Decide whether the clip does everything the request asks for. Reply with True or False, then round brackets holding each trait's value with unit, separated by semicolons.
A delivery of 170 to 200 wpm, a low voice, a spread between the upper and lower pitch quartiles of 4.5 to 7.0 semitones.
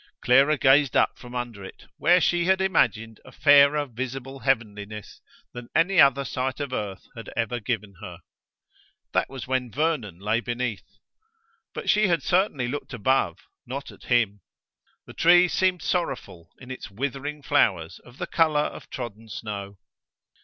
False (155 wpm; 125 Hz; 4.9 semitones)